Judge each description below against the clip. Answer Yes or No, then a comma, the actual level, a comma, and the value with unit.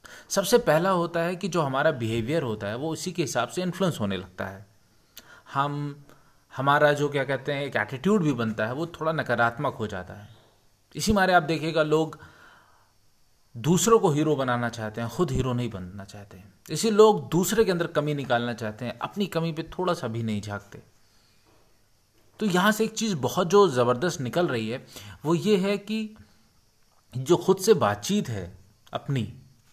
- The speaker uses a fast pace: No, average, 180 wpm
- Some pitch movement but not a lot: No, wide, 7.7 semitones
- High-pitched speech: No, medium, 140 Hz